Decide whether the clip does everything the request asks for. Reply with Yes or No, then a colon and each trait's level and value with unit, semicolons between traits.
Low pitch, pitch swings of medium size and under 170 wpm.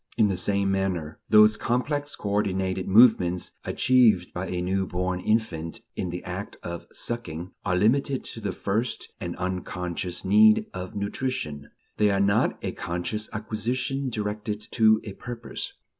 Yes: low, 100 Hz; average, 3.3 semitones; average, 145 wpm